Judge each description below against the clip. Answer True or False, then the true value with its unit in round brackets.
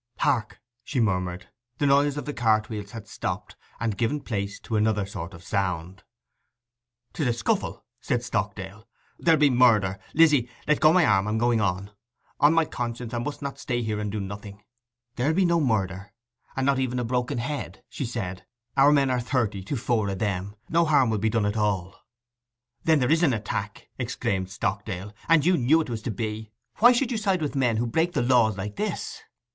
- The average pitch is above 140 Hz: False (115 Hz)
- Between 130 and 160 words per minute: False (200 wpm)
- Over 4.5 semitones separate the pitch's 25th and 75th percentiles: True (5.4 semitones)